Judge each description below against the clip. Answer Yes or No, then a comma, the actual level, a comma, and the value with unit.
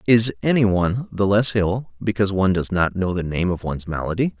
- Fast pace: Yes, fast, 220 wpm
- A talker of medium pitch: No, low, 100 Hz